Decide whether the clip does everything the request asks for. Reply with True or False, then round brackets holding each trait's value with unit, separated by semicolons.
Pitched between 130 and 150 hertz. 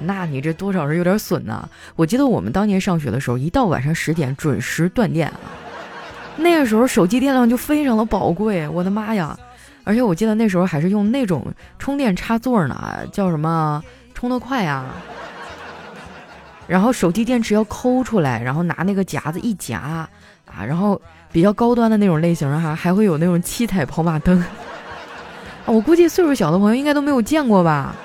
False (190 Hz)